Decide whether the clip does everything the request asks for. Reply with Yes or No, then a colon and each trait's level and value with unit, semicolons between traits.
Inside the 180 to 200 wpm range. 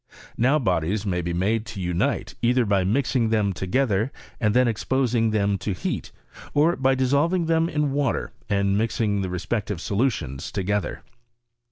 No: average, 160 wpm